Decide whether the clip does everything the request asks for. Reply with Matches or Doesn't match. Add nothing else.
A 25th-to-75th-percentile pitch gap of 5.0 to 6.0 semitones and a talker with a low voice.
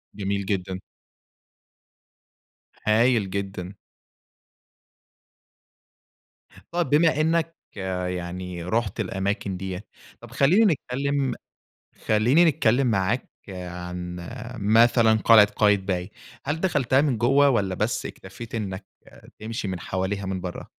Matches